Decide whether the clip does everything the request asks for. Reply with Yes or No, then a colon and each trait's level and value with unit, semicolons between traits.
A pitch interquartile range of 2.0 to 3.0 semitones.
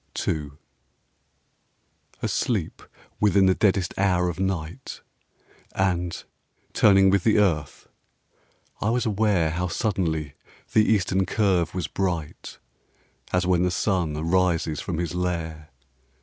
Yes: average, 2.7 semitones